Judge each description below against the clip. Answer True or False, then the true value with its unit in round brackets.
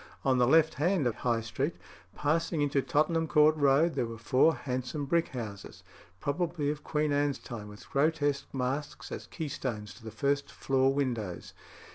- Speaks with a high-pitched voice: False (140 Hz)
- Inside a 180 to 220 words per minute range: False (165 wpm)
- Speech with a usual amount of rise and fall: True (3.4 semitones)